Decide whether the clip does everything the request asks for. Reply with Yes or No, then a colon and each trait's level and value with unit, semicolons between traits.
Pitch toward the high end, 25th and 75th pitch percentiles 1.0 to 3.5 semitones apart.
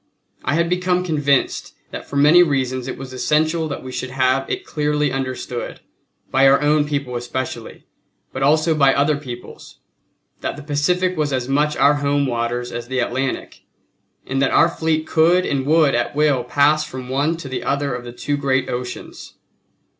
No: medium, 140 Hz; average, 2.8 semitones